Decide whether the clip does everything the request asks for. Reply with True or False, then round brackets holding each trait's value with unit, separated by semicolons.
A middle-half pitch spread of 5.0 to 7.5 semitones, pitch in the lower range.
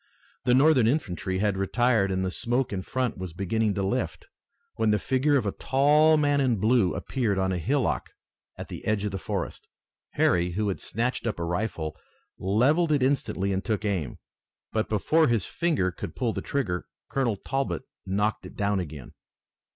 True (5.5 semitones; 110 Hz)